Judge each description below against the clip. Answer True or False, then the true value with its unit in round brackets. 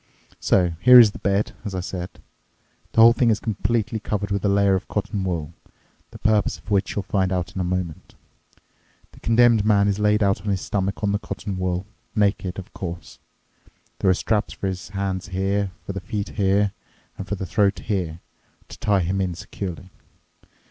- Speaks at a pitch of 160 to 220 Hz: False (100 Hz)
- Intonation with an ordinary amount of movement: False (1.9 semitones)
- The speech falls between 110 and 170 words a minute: False (190 wpm)